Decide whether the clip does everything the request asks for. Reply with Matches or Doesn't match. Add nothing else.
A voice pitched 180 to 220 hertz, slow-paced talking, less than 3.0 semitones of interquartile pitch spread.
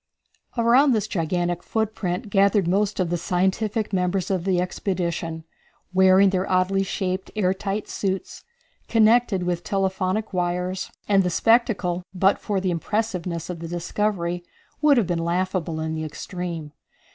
Doesn't match